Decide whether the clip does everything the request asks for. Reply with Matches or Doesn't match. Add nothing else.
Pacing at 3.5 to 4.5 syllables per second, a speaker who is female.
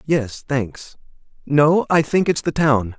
Doesn't match